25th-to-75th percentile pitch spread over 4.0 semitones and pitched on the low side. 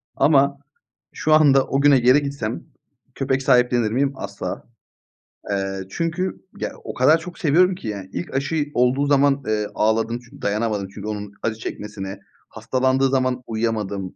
Yes: average, 4.6 semitones; low, 125 Hz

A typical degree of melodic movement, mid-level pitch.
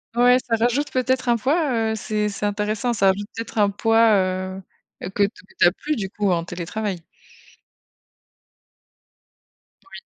No: average, 3.8 semitones; high, 215 Hz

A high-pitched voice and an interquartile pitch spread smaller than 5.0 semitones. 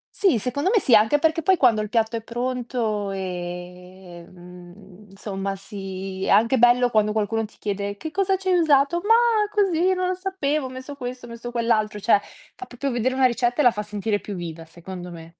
No: high, 225 Hz; wide, 5.6 semitones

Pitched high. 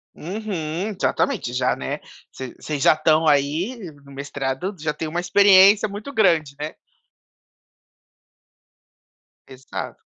No: medium, 155 Hz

